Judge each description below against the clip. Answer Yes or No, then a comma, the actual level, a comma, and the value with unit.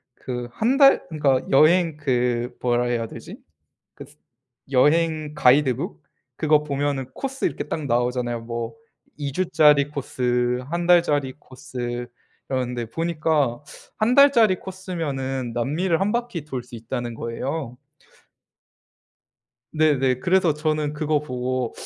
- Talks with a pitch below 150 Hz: Yes, medium, 140 Hz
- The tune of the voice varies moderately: Yes, average, 4.6 semitones